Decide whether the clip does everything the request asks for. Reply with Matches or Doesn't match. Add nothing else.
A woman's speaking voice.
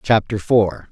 Doesn't match